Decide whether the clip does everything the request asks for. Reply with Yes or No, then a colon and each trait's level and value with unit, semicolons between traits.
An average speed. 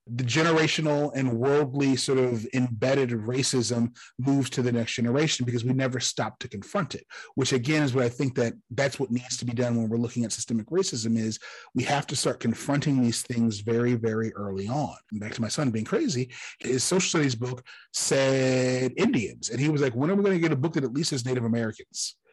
No: fast, 220 wpm